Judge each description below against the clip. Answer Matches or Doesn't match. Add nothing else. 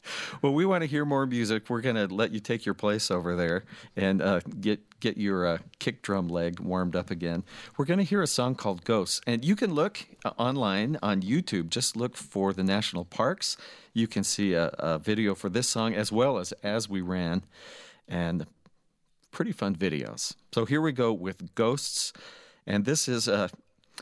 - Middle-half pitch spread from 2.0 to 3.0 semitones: Doesn't match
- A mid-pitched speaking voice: Doesn't match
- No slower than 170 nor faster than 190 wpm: Doesn't match